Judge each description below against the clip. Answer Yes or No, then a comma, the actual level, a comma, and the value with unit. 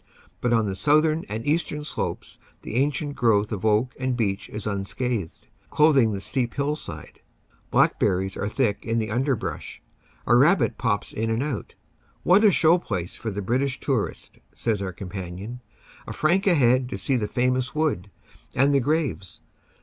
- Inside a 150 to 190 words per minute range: Yes, average, 170 wpm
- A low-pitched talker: Yes, low, 120 Hz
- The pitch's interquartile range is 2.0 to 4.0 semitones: No, wide, 5.6 semitones